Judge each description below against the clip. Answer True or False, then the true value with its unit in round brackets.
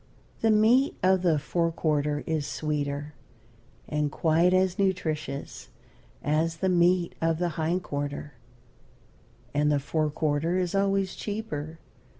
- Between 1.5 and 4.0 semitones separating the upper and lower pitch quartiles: True (3.6 semitones)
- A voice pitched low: False (160 Hz)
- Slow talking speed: True (130 wpm)